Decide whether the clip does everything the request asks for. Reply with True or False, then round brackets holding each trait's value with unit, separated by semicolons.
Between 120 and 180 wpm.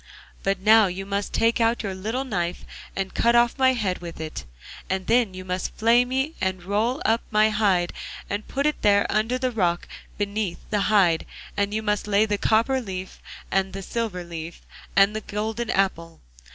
False (190 wpm)